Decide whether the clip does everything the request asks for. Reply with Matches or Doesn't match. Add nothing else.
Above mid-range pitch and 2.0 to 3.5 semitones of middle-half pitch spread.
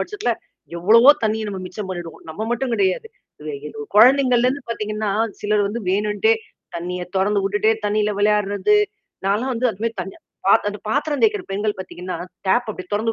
Matches